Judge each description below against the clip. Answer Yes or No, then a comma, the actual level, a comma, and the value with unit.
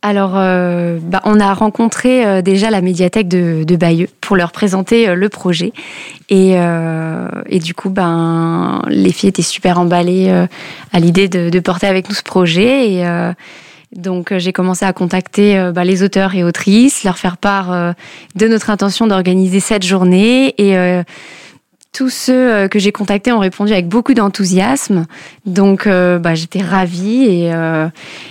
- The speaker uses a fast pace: No, average, 175 wpm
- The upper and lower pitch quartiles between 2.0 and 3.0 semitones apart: Yes, narrow, 2.4 semitones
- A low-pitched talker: No, high, 190 Hz